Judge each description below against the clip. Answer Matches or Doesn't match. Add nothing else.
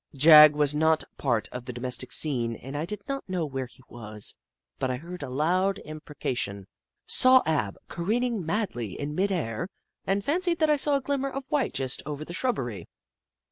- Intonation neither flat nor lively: Doesn't match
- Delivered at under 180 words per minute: Doesn't match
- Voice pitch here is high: Doesn't match